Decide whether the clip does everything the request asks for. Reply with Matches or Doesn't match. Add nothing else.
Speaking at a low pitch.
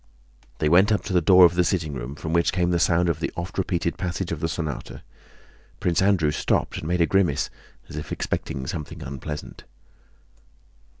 Matches